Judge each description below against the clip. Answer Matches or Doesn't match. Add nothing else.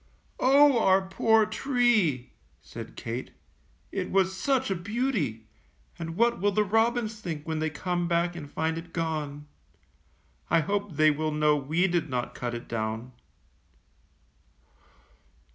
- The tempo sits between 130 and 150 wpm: Matches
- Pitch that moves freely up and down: Matches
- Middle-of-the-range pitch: Matches